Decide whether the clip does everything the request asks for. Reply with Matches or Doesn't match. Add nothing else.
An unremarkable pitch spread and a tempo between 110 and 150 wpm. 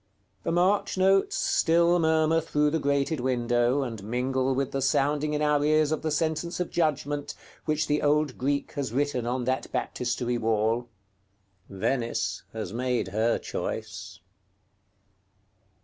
Matches